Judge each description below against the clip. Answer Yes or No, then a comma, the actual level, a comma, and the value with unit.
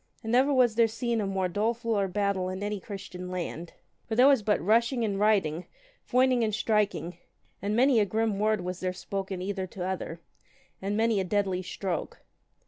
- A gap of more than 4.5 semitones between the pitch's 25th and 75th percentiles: No, average, 3.3 semitones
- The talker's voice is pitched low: No, high, 205 Hz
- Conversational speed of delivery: Yes, average, 185 wpm